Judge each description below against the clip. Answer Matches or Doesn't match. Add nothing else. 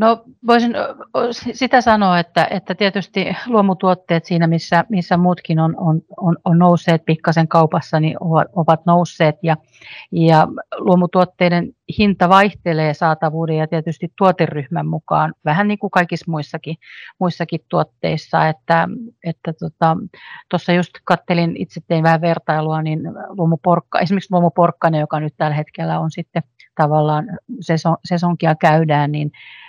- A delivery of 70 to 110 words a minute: Doesn't match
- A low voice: Doesn't match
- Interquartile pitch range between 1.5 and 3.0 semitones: Matches